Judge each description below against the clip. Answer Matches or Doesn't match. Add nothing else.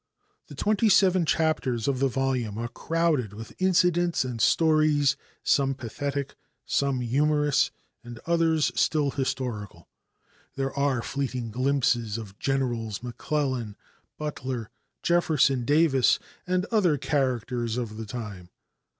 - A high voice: Doesn't match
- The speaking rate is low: Matches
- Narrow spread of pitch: Doesn't match